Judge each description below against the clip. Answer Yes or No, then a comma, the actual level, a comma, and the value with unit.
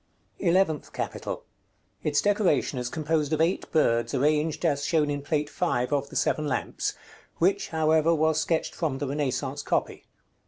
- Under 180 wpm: Yes, average, 155 wpm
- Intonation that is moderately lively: No, narrow, 2.2 semitones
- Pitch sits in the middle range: Yes, medium, 150 Hz